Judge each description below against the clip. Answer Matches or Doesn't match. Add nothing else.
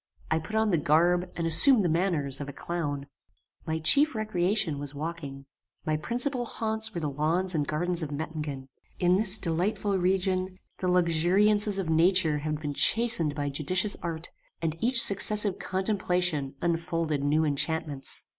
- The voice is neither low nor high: Matches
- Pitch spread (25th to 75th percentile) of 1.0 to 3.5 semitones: Doesn't match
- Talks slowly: Doesn't match